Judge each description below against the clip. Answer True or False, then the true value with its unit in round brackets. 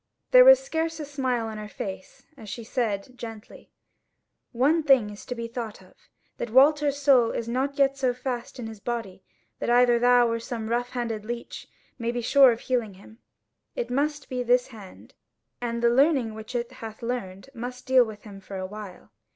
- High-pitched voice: True (240 Hz)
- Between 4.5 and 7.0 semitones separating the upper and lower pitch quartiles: False (2.9 semitones)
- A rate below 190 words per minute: False (200 wpm)